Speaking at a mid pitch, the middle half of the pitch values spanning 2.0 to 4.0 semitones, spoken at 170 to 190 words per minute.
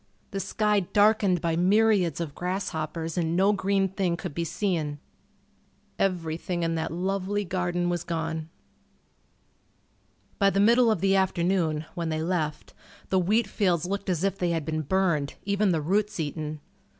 No: medium, 180 Hz; average, 3.3 semitones; average, 155 wpm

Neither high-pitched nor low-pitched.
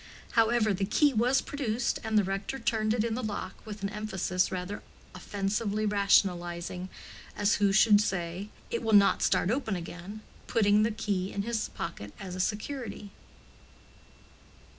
No: high, 205 Hz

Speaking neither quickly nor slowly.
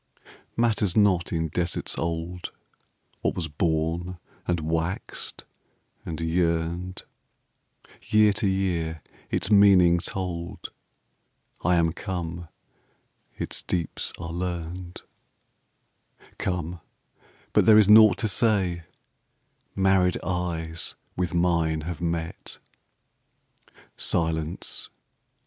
No: slow, 90 wpm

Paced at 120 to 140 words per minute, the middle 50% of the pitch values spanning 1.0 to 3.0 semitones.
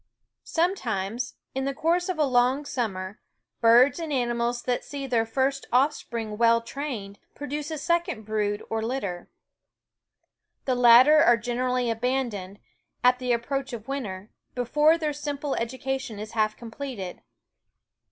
No: slow, 135 wpm; average, 3.7 semitones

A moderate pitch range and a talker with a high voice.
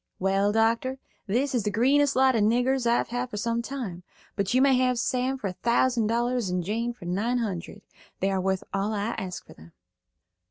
Yes: average, 4.3 semitones; high, 230 Hz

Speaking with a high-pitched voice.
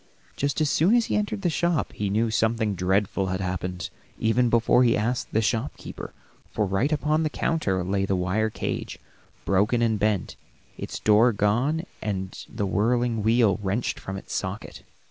No: low, 110 Hz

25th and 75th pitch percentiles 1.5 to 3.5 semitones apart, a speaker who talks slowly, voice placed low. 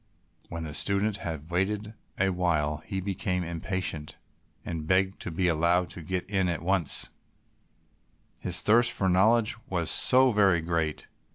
No: average, 2.8 semitones; average, 150 wpm; very low, 90 Hz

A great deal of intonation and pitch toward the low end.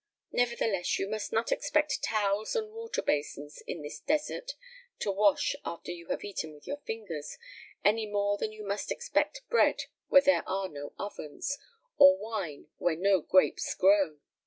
No: wide, 6.7 semitones; high, 205 Hz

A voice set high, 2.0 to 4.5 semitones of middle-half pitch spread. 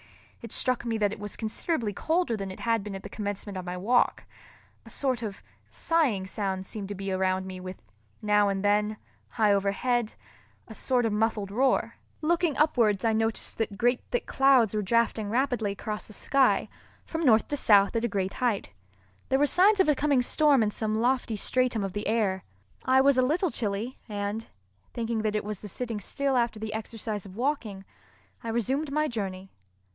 Yes: high, 220 Hz; average, 3.8 semitones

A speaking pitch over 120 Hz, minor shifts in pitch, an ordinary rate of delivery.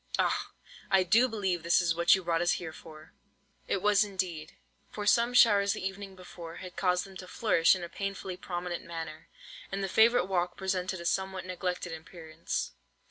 Yes: medium, 185 Hz; narrow, 2.3 semitones; average, 190 wpm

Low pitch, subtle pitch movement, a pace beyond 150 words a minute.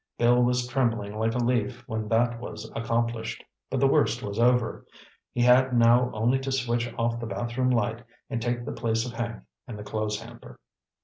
Yes: low, 120 Hz; narrow, 1.5 semitones; average, 190 wpm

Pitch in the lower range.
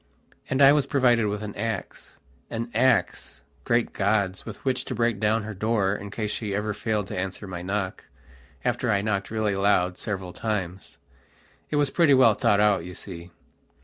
Yes: low, 105 Hz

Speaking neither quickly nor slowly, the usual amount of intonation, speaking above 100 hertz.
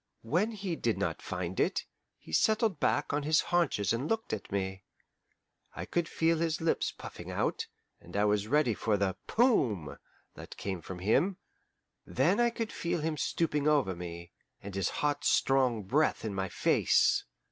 No: average, 170 wpm; wide, 9.0 semitones; low, 135 Hz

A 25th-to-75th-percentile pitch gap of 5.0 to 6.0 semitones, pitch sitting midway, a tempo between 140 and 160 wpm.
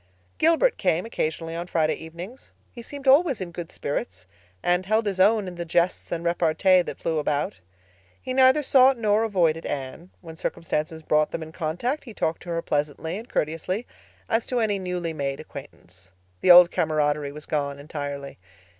No: wide, 5.4 semitones; medium, 170 Hz; average, 175 wpm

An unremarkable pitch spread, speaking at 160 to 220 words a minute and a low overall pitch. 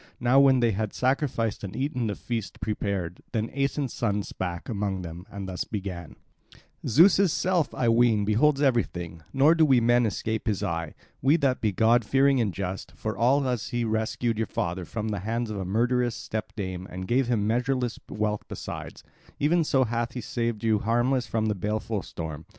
Yes: average, 3.8 semitones; average, 185 wpm; low, 115 Hz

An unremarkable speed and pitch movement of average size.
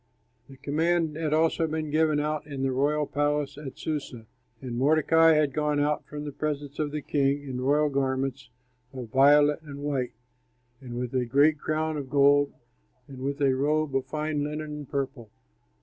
No: average, 180 wpm; narrow, 2.0 semitones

